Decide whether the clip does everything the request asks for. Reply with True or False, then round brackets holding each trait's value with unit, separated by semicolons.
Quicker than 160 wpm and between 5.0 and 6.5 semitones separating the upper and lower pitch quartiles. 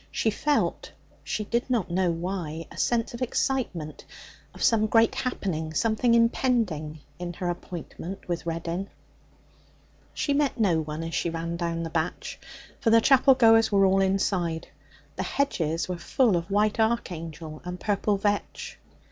False (155 wpm; 5.3 semitones)